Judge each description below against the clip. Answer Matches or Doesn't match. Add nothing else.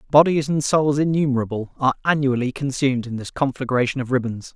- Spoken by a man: Matches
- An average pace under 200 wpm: Matches